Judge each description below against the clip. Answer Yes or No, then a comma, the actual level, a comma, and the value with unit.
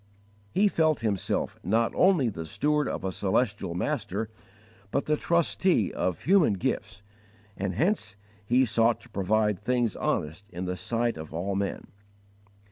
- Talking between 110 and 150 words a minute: Yes, average, 145 wpm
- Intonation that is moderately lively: No, wide, 5.7 semitones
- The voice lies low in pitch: Yes, low, 110 Hz